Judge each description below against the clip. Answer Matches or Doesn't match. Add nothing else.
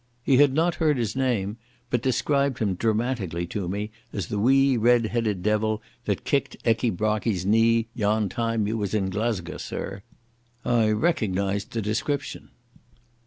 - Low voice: Matches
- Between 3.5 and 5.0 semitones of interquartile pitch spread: Doesn't match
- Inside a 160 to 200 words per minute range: Doesn't match